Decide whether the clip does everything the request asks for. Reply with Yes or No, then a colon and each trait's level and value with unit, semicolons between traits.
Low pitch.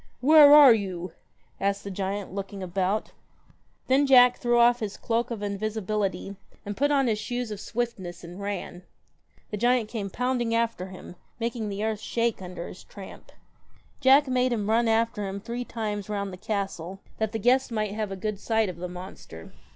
No: high, 215 Hz